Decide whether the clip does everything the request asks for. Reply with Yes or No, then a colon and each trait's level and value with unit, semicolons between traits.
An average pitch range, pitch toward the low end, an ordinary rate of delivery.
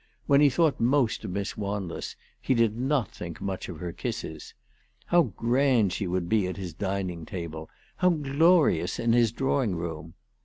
No: wide, 7.1 semitones; low, 105 Hz; average, 170 wpm